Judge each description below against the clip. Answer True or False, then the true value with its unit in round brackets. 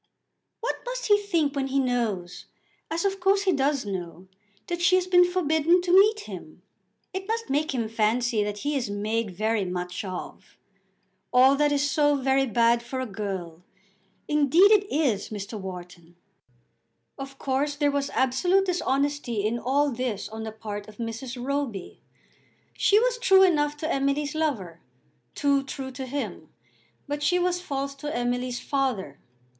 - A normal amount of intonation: False (6.0 semitones)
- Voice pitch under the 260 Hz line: False (270 Hz)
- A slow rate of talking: False (160 wpm)